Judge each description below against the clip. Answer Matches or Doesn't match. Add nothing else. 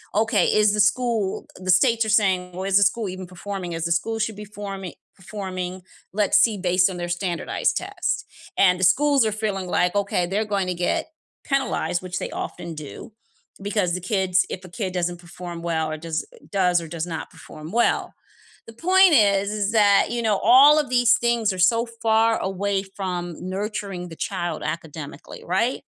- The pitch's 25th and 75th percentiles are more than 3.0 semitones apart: Matches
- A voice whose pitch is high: Matches